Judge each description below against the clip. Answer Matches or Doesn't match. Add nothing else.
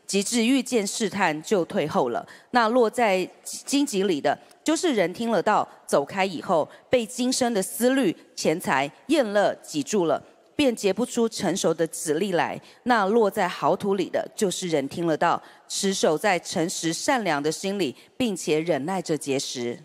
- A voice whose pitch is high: Matches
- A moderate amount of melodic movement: Doesn't match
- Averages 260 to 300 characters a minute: Doesn't match